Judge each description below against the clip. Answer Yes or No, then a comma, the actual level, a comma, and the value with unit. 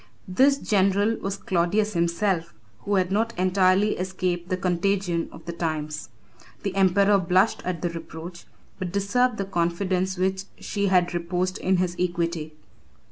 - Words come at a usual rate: Yes, average, 145 wpm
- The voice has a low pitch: No, medium, 185 Hz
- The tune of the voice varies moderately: No, narrow, 2.3 semitones